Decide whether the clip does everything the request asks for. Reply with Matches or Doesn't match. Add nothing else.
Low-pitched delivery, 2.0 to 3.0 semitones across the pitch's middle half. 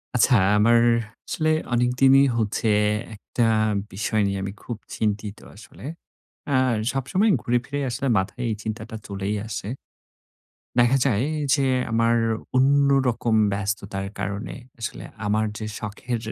Doesn't match